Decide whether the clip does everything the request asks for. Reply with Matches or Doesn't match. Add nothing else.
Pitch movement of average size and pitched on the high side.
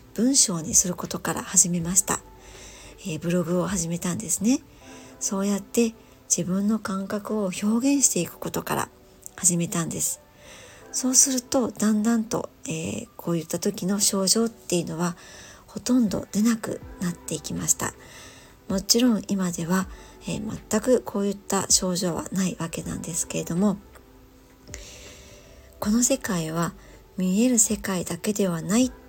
Matches